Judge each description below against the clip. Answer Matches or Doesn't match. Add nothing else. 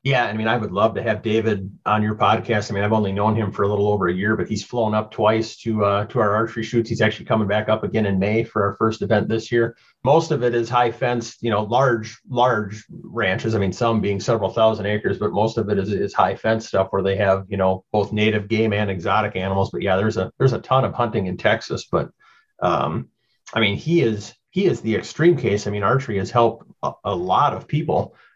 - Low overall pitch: Matches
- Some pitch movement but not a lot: Doesn't match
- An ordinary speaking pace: Doesn't match